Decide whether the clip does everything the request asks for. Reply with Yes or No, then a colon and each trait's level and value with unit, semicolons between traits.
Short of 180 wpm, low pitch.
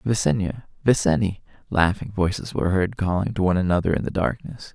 Yes: average, 165 wpm; very low, 95 Hz